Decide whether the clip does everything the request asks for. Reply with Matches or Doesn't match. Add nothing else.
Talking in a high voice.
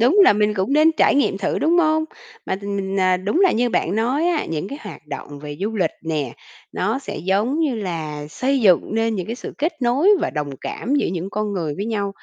Matches